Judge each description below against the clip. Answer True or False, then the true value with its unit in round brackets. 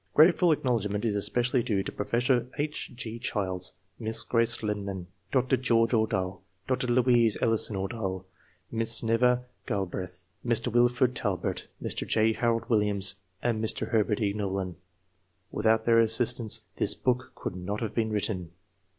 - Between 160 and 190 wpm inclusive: False (140 wpm)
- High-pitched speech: False (115 Hz)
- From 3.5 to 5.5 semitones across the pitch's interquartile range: False (3.0 semitones)